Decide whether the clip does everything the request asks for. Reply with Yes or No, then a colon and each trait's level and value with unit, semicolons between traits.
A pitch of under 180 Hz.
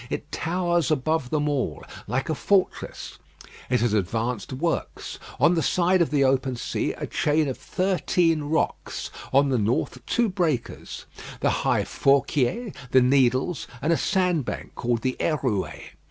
Yes: medium, 140 Hz